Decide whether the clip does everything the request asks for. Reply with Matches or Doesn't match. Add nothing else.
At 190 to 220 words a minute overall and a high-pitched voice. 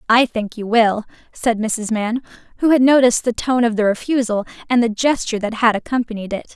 Matches